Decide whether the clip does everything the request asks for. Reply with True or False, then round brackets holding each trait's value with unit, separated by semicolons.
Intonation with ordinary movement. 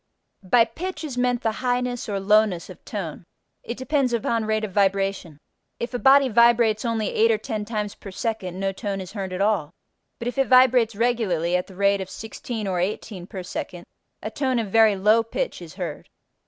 True (3.6 semitones)